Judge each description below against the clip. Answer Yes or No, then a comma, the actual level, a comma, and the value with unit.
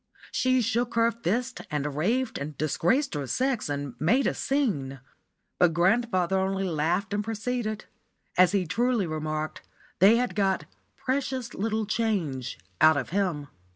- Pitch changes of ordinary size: No, wide, 7.0 semitones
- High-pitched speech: Yes, high, 195 Hz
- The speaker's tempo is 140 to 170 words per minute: Yes, average, 145 wpm